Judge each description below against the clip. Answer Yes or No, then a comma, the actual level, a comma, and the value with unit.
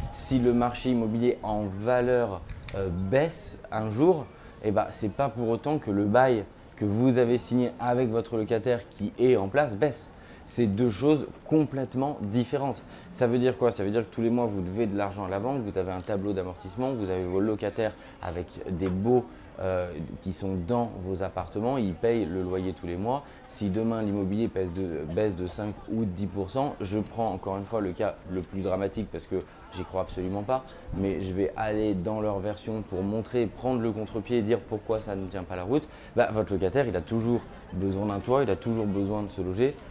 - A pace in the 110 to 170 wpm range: No, average, 215 wpm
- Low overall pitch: Yes, low, 105 Hz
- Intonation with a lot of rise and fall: No, average, 4.1 semitones